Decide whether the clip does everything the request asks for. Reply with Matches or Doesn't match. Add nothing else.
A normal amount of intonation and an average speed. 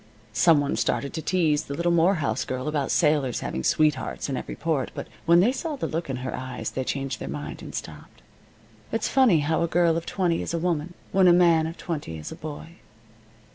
Doesn't match